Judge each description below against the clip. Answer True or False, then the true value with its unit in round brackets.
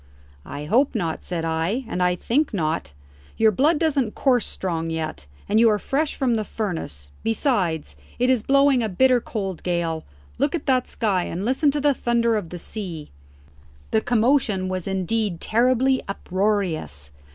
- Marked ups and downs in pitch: True (6.6 semitones)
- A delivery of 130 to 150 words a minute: False (165 wpm)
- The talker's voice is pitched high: True (215 Hz)